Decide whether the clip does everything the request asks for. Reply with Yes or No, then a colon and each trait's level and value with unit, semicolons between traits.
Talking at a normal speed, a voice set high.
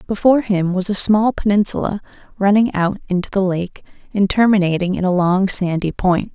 Yes: average, 170 wpm; high, 195 Hz